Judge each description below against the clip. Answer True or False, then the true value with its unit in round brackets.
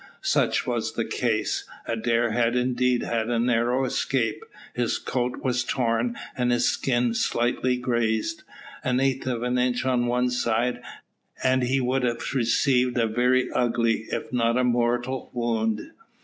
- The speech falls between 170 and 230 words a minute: False (150 wpm)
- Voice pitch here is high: False (120 Hz)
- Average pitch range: False (1.3 semitones)